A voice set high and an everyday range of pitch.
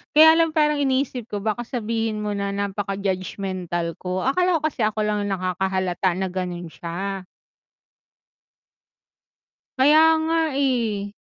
No: high, 205 Hz; wide, 5.7 semitones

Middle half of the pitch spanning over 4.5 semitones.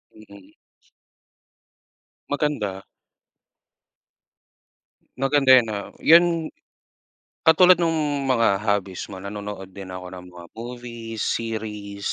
Yes: average, 5.3 semitones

